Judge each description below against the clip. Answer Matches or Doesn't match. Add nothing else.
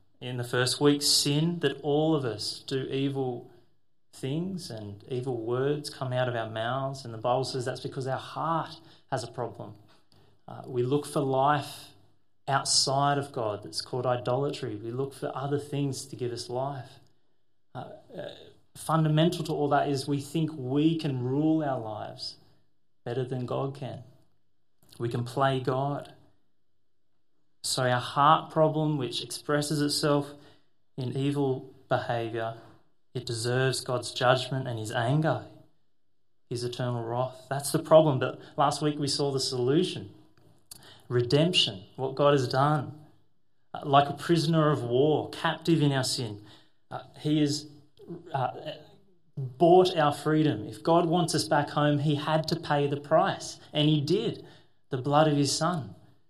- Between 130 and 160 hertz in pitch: Matches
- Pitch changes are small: Doesn't match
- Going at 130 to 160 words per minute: Matches